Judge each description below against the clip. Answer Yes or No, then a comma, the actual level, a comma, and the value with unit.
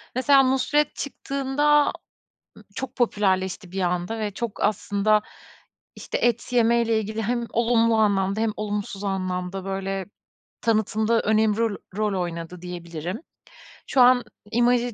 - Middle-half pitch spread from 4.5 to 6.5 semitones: No, average, 3.8 semitones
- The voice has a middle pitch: No, high, 215 Hz